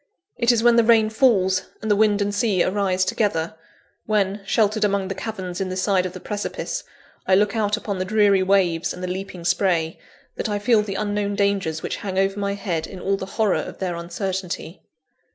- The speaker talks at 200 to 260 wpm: Yes, fast, 205 wpm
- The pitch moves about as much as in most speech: No, narrow, 2.1 semitones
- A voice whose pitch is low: No, high, 195 Hz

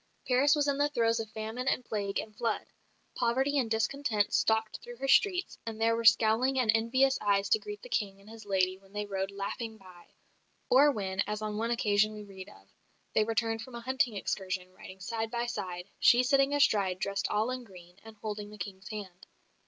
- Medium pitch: No, high, 220 Hz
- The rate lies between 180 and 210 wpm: Yes, fast, 205 wpm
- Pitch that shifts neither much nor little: Yes, average, 3.8 semitones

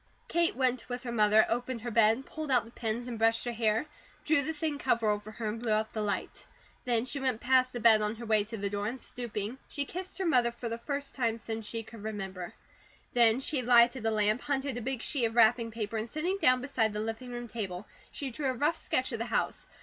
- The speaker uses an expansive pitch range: No, average, 2.8 semitones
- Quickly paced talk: Yes, fast, 245 wpm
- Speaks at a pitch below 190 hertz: No, high, 235 Hz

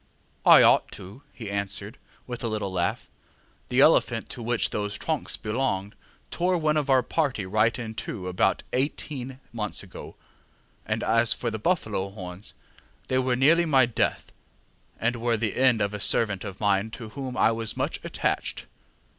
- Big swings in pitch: No, average, 4.1 semitones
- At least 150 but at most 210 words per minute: Yes, average, 170 wpm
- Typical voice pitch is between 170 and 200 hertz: No, low, 115 Hz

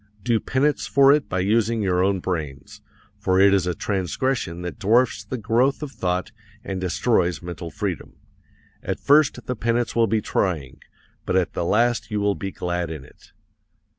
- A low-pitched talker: Yes, low, 100 Hz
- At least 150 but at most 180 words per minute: Yes, average, 175 wpm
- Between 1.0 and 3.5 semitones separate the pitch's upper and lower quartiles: No, average, 4.8 semitones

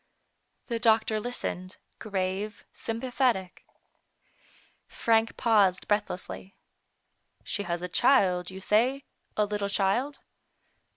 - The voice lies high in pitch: Yes, high, 210 Hz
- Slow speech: Yes, slow, 105 wpm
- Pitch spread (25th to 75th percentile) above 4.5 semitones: No, average, 3.4 semitones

